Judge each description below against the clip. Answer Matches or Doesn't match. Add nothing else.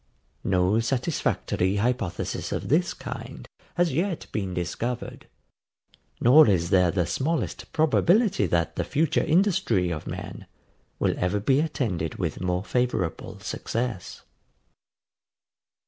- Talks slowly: Matches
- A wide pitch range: Matches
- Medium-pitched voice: Doesn't match